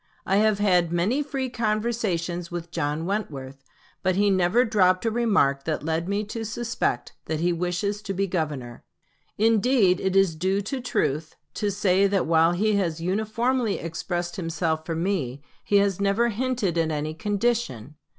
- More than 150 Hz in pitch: Yes, high, 190 Hz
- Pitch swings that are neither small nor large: Yes, average, 4.5 semitones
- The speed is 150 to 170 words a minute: Yes, average, 165 wpm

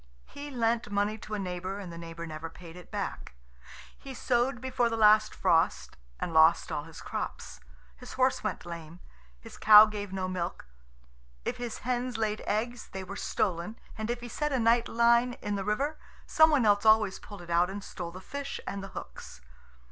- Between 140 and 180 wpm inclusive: No, average, 195 wpm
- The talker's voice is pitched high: Yes, high, 210 Hz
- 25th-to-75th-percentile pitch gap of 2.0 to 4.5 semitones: No, average, 4.9 semitones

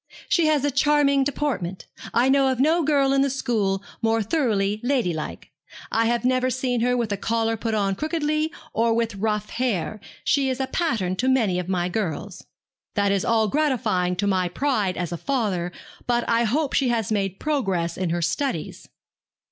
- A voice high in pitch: Yes, high, 230 Hz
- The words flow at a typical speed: Yes, average, 185 wpm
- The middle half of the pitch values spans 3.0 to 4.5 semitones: No, wide, 5.6 semitones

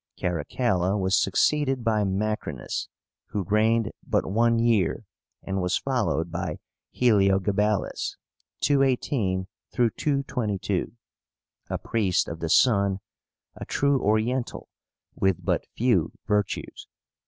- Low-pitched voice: Yes, low, 105 Hz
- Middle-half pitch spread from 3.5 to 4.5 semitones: Yes, average, 3.8 semitones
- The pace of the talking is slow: Yes, slow, 100 wpm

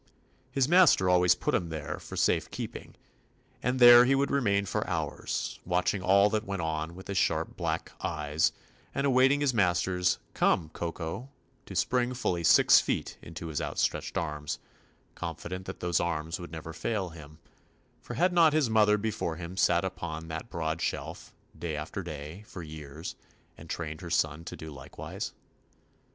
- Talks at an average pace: Yes, average, 175 wpm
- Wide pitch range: No, average, 4.8 semitones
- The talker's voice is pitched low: Yes, very low, 90 Hz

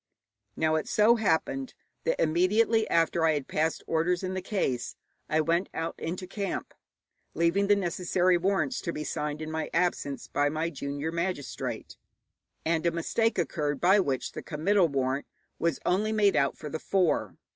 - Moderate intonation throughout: Yes, average, 3.7 semitones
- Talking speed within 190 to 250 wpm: No, average, 165 wpm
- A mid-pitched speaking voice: Yes, medium, 170 Hz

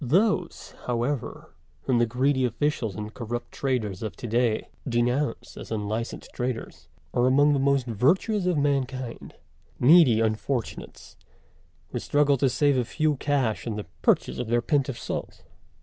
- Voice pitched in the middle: No, low, 125 Hz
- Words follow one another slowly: No, average, 150 wpm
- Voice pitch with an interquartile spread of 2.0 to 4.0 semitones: Yes, average, 3.6 semitones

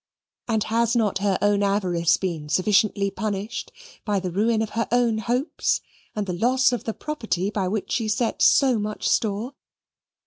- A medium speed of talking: Yes, average, 170 wpm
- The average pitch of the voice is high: Yes, high, 215 Hz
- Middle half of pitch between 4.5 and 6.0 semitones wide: No, average, 2.8 semitones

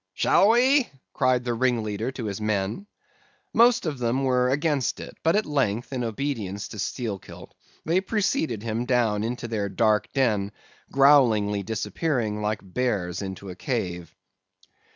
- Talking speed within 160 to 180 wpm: No, average, 145 wpm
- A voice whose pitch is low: Yes, low, 120 Hz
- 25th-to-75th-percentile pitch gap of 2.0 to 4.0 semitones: No, average, 4.7 semitones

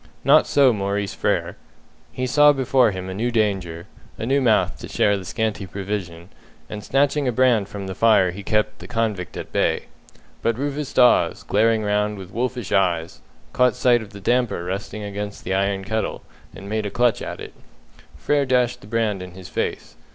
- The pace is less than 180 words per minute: No, average, 190 wpm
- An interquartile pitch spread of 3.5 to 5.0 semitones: Yes, average, 3.9 semitones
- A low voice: Yes, low, 105 Hz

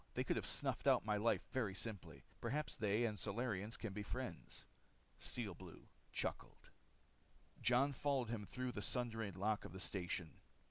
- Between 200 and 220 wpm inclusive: No, average, 165 wpm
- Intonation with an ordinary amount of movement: Yes, average, 3.9 semitones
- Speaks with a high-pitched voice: No, low, 110 Hz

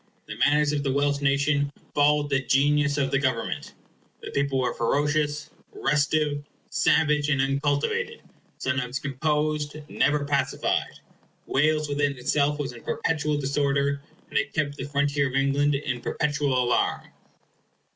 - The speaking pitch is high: No, medium, 145 Hz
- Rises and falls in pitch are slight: Yes, narrow, 1.3 semitones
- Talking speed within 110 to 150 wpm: Yes, slow, 135 wpm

